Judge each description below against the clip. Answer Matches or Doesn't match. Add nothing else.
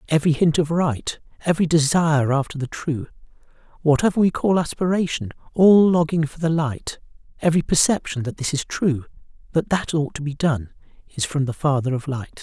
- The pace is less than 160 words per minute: Doesn't match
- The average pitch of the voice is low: Doesn't match